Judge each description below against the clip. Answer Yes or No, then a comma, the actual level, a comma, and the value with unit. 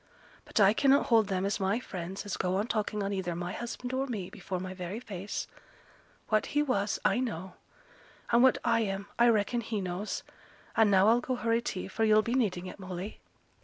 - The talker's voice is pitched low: No, high, 205 Hz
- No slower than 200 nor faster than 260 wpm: Yes, fast, 205 wpm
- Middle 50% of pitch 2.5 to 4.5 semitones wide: Yes, average, 3.7 semitones